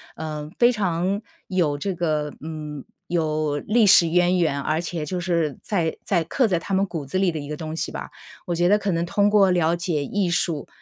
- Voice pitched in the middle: Yes, medium, 170 Hz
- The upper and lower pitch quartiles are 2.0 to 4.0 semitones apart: Yes, average, 3.4 semitones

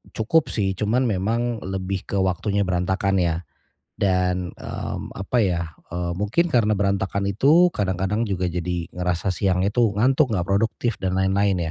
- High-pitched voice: No, very low, 95 Hz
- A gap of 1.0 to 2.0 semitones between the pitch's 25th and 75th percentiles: No, average, 2.7 semitones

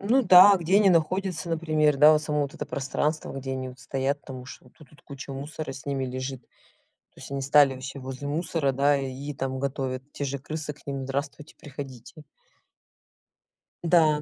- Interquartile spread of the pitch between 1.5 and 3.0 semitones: Yes, narrow, 2.5 semitones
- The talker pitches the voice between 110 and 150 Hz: Yes, medium, 140 Hz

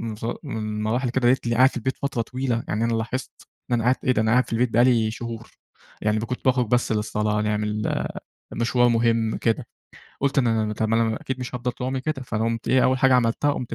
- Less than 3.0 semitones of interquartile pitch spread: Yes, narrow, 2.5 semitones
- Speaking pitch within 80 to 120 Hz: Yes, low, 115 Hz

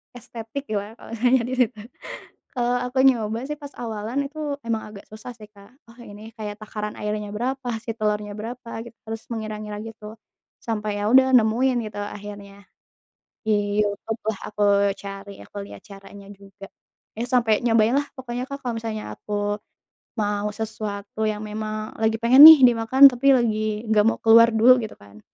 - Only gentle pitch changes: Yes, narrow, 2.3 semitones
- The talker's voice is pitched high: Yes, high, 220 Hz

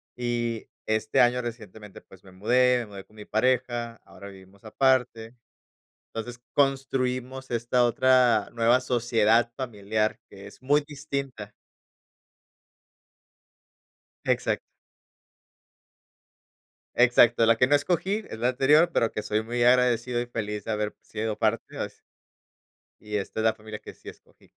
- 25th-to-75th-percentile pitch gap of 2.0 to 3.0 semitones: Yes, narrow, 2.6 semitones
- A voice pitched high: No, low, 120 Hz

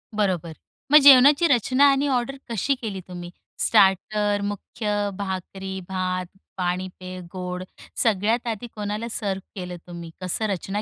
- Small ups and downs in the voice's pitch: No, average, 3.7 semitones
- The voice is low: No, high, 200 Hz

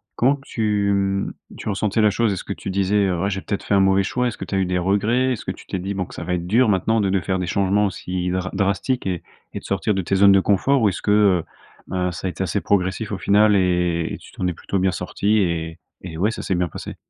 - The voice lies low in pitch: Yes, very low, 95 Hz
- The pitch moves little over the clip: Yes, narrow, 2.2 semitones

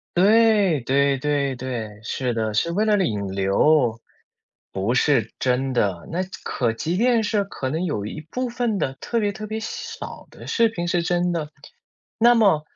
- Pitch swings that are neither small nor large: No, wide, 8.7 semitones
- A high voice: No, medium, 155 Hz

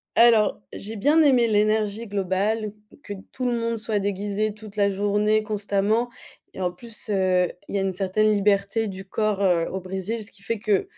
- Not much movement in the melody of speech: Yes, narrow, 1.9 semitones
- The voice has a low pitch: No, high, 205 Hz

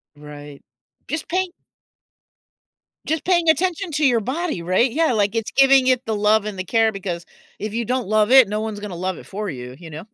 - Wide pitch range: Yes, wide, 6.2 semitones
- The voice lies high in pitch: Yes, high, 220 Hz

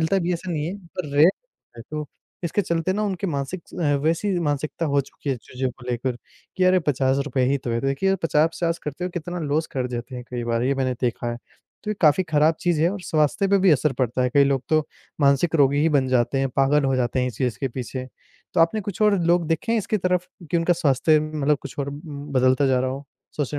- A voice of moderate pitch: Yes, medium, 145 Hz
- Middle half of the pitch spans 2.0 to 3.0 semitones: No, average, 4.5 semitones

